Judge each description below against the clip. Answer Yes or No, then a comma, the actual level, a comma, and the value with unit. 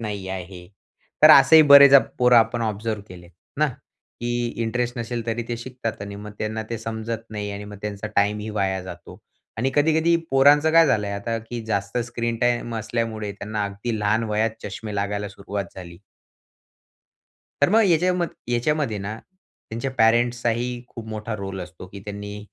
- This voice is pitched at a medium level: No, low, 110 Hz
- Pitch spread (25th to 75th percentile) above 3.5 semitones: No, average, 3.0 semitones